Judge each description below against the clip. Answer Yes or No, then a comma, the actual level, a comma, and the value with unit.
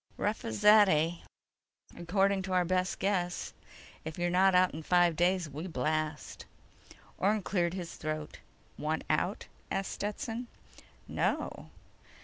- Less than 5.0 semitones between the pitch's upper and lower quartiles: Yes, average, 3.4 semitones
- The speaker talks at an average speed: No, slow, 130 wpm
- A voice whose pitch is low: No, medium, 180 Hz